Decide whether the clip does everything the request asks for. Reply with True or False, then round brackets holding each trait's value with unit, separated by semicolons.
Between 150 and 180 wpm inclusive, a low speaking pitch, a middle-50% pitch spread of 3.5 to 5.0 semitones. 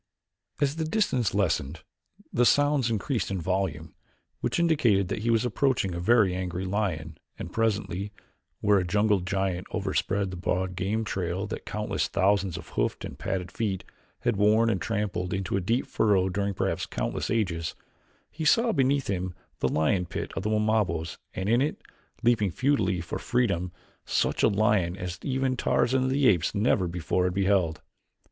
True (170 wpm; 100 Hz; 4.0 semitones)